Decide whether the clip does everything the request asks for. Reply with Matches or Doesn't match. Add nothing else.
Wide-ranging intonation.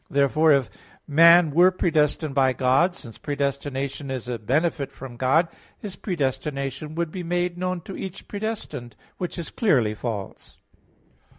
Doesn't match